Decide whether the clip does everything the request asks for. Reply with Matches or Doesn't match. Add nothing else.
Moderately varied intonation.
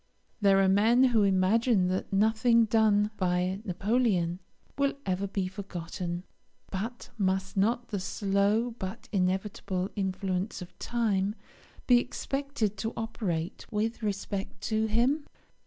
Matches